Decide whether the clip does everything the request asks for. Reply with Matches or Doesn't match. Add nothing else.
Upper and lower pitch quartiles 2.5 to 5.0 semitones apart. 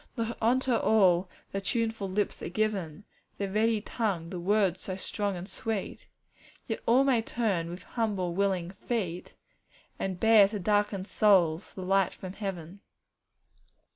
Matches